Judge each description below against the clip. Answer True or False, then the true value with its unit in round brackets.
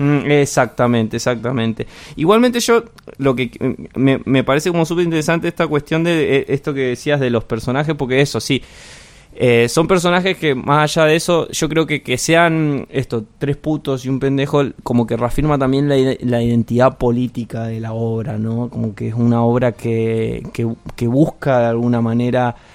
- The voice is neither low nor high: False (130 Hz)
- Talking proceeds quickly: False (180 wpm)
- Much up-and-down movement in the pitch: False (4.1 semitones)